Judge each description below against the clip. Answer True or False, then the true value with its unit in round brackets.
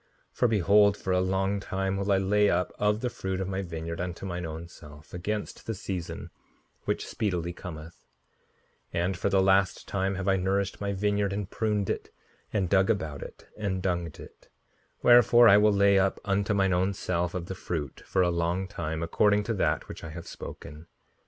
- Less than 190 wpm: False (195 wpm)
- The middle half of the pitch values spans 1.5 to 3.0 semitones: True (2.5 semitones)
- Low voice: True (95 Hz)